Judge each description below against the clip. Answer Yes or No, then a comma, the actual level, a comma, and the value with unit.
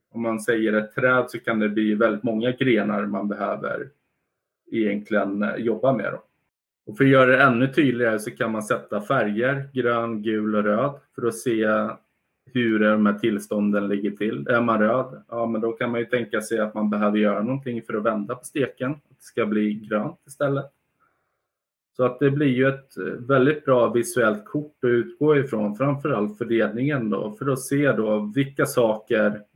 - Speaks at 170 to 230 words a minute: Yes, average, 185 wpm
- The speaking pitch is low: Yes, low, 115 Hz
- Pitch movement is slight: No, average, 3.8 semitones